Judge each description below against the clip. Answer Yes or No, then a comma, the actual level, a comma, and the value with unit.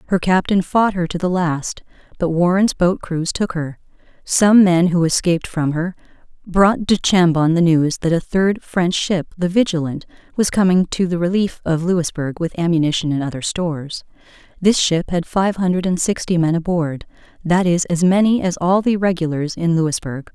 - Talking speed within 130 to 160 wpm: No, average, 185 wpm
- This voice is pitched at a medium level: Yes, medium, 175 Hz